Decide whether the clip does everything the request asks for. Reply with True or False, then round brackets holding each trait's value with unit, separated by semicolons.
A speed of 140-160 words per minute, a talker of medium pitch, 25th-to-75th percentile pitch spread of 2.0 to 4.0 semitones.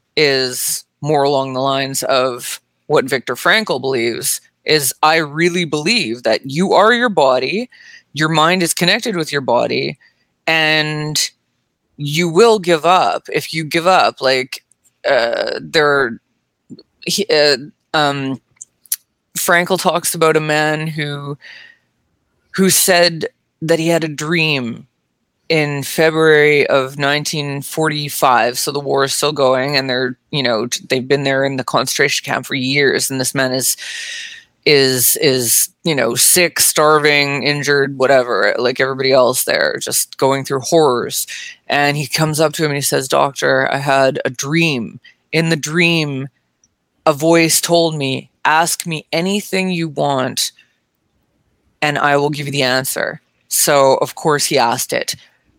True (145 wpm; 150 Hz; 3.5 semitones)